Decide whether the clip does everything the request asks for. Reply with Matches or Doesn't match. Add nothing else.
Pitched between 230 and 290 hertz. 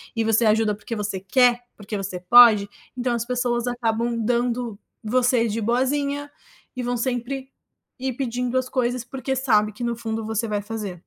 Matches